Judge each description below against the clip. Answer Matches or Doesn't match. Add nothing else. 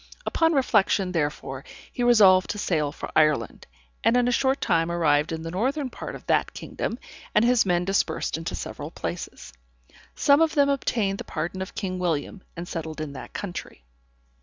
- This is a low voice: Doesn't match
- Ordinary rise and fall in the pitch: Doesn't match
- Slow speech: Doesn't match